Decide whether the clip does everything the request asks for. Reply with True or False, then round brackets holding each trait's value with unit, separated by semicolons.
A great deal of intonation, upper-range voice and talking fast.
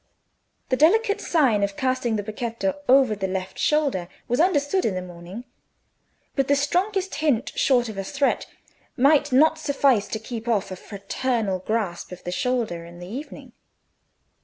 False (6.2 semitones; 245 Hz; 160 wpm)